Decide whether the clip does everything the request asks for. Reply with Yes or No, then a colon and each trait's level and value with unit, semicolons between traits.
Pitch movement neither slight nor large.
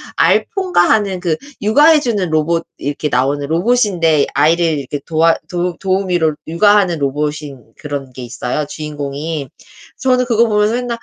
No: wide, 6.0 semitones